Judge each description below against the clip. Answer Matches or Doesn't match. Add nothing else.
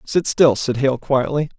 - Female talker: Doesn't match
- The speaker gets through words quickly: Doesn't match